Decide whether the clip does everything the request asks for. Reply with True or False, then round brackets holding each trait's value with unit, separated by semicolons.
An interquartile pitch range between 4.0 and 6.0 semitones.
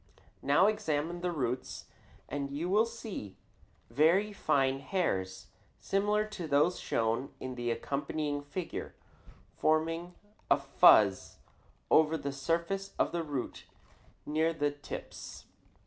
True (4.3 semitones)